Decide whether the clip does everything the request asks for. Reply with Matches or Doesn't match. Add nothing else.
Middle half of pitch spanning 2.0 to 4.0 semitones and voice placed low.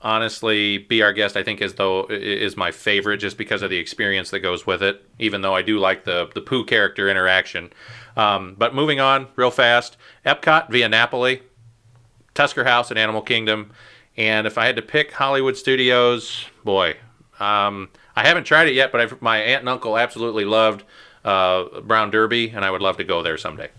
Matches